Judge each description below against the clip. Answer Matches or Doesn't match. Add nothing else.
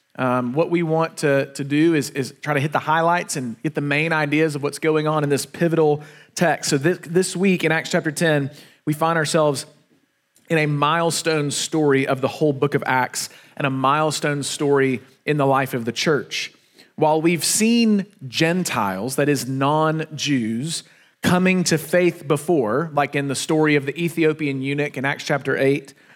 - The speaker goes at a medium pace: Matches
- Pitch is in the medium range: Matches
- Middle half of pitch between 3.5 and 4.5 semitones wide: Doesn't match